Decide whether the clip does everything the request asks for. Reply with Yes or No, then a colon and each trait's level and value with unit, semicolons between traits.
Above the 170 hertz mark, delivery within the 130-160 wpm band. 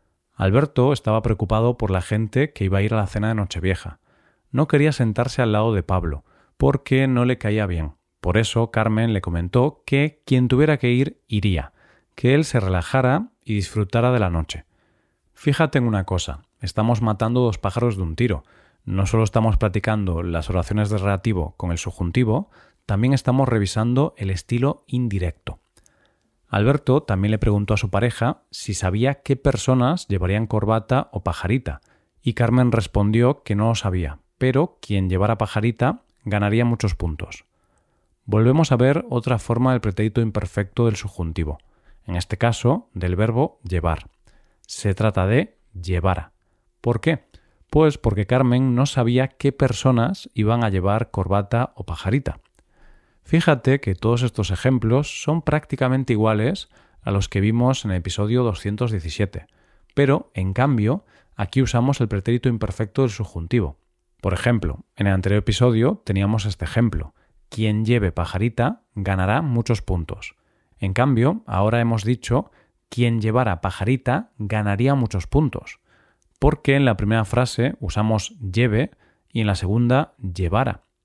No: low, 110 Hz; average, 150 wpm